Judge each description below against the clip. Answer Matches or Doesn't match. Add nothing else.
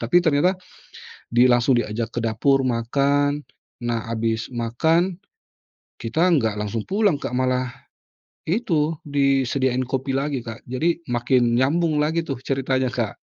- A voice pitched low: Matches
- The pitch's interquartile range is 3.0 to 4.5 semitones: Matches